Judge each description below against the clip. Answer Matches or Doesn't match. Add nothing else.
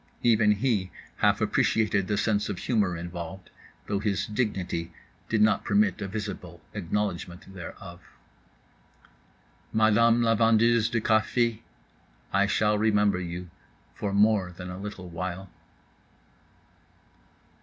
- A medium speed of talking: Doesn't match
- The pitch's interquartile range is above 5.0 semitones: Doesn't match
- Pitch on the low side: Matches